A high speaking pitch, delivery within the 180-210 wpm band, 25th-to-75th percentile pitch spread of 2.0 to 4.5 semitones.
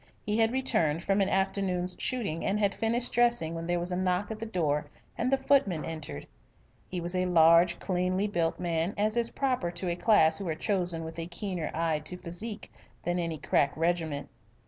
No: medium, 180 Hz; average, 200 wpm; average, 3.9 semitones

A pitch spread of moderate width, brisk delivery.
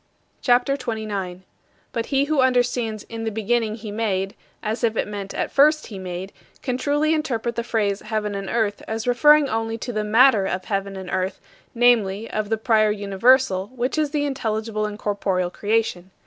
No: average, 3.4 semitones; average, 185 wpm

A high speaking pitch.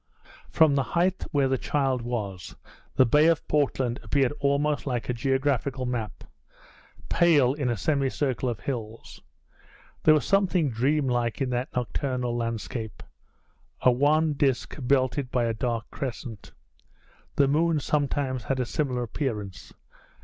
No: low, 130 Hz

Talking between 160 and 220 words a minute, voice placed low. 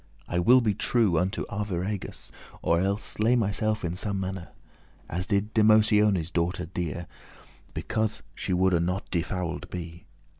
No: average, 140 wpm; very low, 95 Hz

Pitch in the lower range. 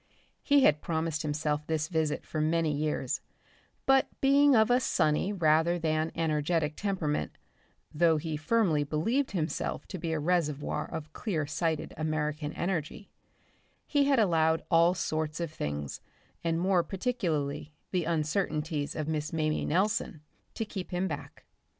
No: medium, 160 Hz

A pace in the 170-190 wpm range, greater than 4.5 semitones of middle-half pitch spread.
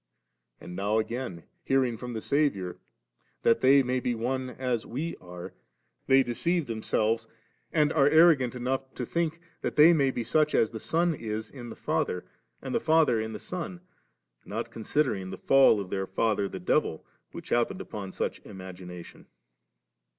Yes: average, 180 wpm; average, 5.2 semitones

